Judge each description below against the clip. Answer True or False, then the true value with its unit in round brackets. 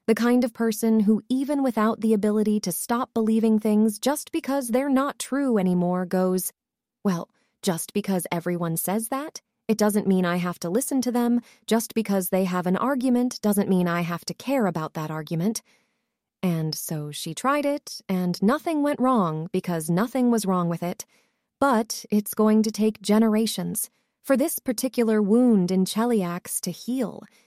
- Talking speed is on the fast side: False (175 wpm)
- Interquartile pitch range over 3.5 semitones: True (4.8 semitones)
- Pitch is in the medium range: False (220 Hz)